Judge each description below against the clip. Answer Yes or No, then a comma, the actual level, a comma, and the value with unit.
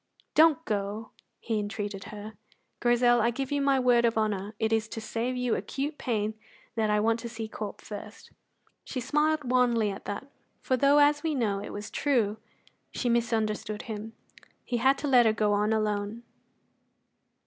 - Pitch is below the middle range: No, high, 225 Hz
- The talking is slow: No, average, 175 wpm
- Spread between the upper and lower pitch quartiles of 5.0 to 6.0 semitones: No, average, 3.2 semitones